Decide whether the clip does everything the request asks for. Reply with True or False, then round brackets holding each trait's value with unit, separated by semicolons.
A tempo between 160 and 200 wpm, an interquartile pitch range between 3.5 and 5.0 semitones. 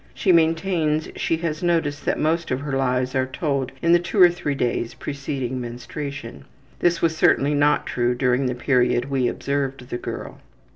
True (180 wpm; 4.1 semitones)